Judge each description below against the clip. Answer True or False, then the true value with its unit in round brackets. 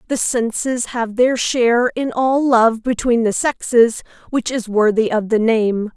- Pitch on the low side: False (235 Hz)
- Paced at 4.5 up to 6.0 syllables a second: False (4.1 syllables/s)